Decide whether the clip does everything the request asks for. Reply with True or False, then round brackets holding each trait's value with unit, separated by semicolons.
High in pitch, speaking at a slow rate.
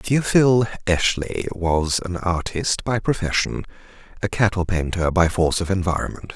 False (95 Hz; 130 wpm)